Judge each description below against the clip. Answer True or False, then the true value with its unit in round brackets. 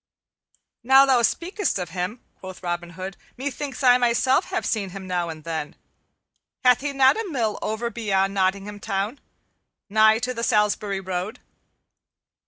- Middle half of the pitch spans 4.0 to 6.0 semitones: True (5.1 semitones)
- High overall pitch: True (215 Hz)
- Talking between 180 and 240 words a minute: False (150 wpm)